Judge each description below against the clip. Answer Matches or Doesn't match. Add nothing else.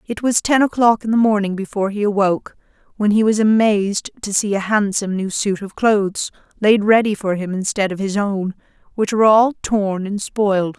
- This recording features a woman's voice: Matches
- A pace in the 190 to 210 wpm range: Matches